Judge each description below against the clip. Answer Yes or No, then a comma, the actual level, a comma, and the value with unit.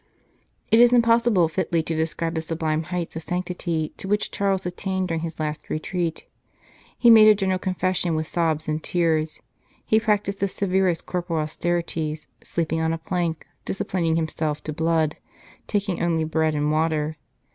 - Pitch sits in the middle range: Yes, medium, 165 Hz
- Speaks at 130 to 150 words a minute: No, average, 165 wpm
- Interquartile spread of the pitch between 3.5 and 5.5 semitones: No, average, 2.9 semitones